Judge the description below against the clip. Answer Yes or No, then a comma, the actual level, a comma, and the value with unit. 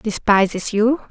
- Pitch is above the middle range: Yes, high, 215 Hz